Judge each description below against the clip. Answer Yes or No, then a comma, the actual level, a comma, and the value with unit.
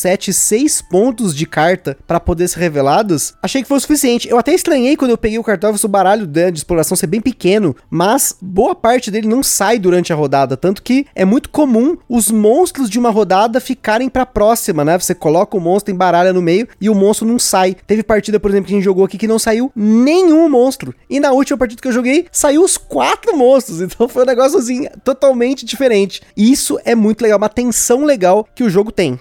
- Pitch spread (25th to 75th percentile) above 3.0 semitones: Yes, average, 5.3 semitones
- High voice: Yes, high, 220 Hz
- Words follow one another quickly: Yes, fast, 225 wpm